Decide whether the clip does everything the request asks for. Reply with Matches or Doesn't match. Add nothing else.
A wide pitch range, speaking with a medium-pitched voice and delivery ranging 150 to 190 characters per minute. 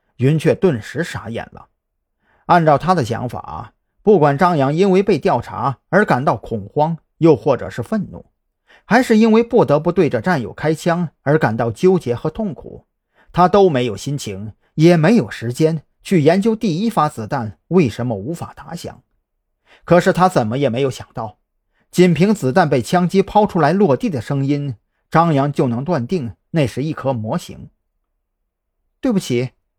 Doesn't match